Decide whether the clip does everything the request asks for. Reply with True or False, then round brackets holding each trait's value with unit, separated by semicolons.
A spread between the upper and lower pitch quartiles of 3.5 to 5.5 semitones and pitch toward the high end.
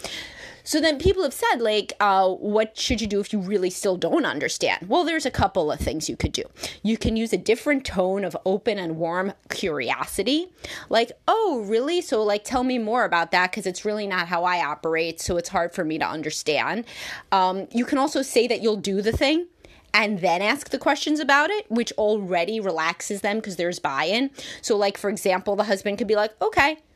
True (5.2 semitones; 210 Hz)